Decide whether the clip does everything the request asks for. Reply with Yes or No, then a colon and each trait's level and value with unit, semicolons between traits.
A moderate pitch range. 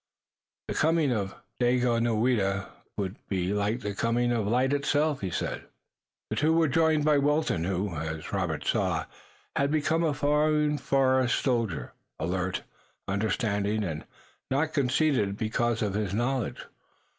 No: wide, 6.2 semitones